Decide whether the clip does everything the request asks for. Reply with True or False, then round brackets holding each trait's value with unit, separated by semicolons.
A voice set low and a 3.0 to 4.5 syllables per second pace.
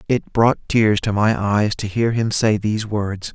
True (105 Hz; 4.2 syllables/s)